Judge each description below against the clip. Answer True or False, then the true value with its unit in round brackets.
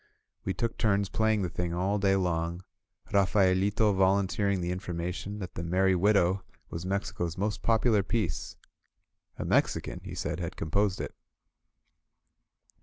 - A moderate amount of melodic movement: False (2.3 semitones)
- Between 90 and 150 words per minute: True (135 wpm)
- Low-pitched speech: True (95 Hz)